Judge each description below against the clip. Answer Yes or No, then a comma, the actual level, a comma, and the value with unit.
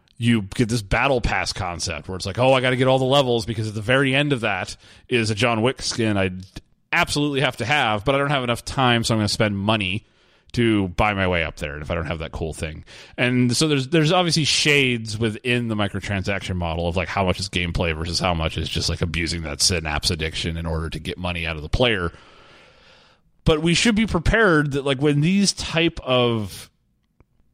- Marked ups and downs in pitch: Yes, wide, 6.8 semitones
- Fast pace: Yes, fast, 230 wpm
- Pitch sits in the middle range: No, low, 110 Hz